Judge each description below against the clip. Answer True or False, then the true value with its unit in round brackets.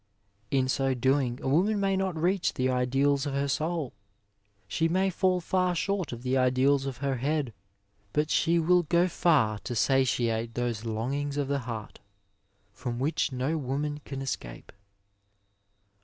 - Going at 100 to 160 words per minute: True (155 wpm)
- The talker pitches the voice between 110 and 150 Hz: True (140 Hz)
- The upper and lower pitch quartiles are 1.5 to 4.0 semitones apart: False (4.5 semitones)